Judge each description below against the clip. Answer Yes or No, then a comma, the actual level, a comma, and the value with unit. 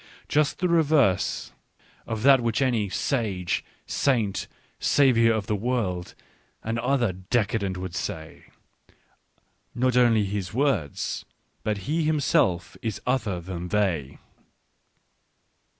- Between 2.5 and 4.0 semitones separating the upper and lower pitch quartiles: No, wide, 5.4 semitones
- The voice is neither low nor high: No, low, 110 Hz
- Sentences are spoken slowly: Yes, slow, 120 wpm